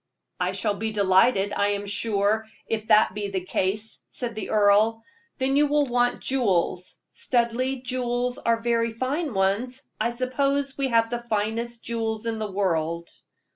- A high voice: Yes, high, 225 Hz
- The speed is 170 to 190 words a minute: No, average, 160 wpm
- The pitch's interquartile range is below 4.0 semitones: Yes, average, 3.3 semitones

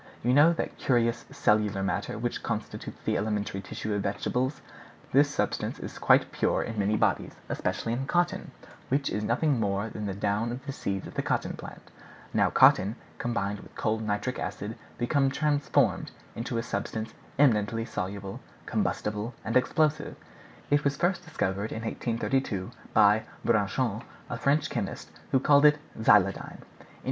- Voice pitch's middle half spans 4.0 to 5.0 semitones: Yes, average, 4.7 semitones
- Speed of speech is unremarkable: Yes, average, 155 wpm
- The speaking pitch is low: Yes, low, 115 Hz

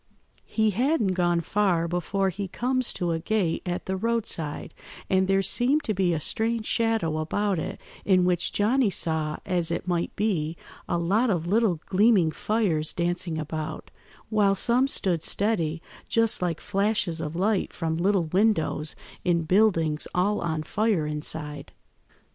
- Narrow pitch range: No, average, 4.5 semitones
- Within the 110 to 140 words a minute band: No, average, 155 wpm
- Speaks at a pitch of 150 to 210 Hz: Yes, medium, 185 Hz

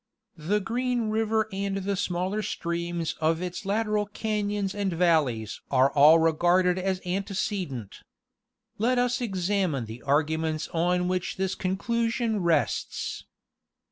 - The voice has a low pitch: No, medium, 185 Hz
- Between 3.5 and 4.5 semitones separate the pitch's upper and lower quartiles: Yes, average, 4.1 semitones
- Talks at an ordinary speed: No, slow, 130 wpm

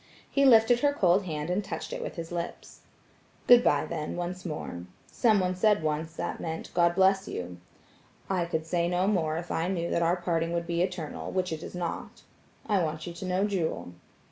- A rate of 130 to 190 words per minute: No, average, 200 wpm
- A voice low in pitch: No, medium, 175 Hz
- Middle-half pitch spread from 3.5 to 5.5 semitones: No, average, 2.7 semitones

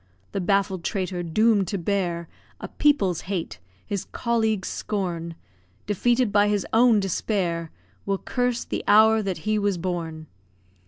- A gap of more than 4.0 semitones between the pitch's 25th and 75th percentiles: No, average, 3.5 semitones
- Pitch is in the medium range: No, high, 195 Hz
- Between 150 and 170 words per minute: No, average, 140 wpm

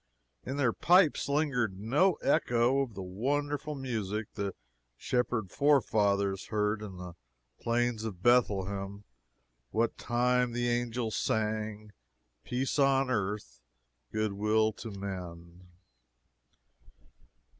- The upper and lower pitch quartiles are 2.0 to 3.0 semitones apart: No, average, 3.7 semitones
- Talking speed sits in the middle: No, slow, 105 wpm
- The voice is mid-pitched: No, low, 110 Hz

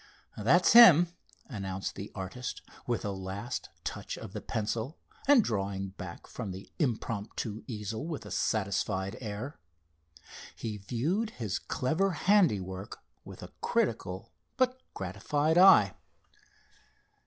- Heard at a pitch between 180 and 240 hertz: No, low, 110 Hz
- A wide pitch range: Yes, wide, 8.0 semitones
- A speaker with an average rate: No, slow, 120 wpm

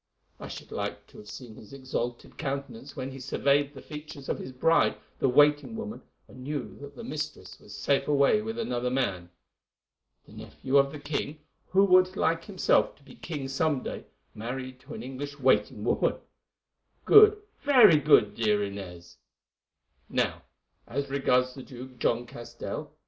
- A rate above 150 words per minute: Yes, average, 165 wpm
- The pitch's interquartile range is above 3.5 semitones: No, average, 3.2 semitones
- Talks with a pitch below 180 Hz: Yes, medium, 140 Hz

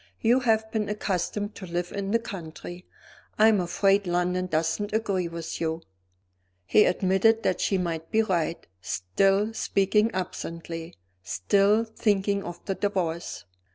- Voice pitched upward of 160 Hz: Yes, high, 190 Hz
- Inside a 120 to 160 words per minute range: Yes, average, 140 wpm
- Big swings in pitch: No, average, 3.5 semitones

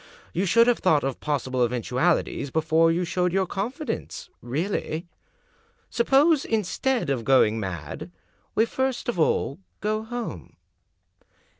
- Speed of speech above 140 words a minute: No, slow, 135 wpm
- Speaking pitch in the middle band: Yes, medium, 175 Hz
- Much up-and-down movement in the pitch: Yes, wide, 8.8 semitones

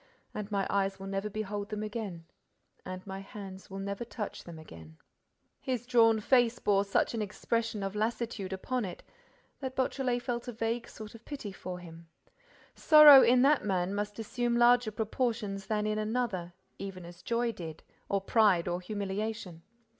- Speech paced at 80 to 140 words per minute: No, average, 170 wpm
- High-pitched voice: Yes, high, 210 Hz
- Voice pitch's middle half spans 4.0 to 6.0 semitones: No, average, 3.5 semitones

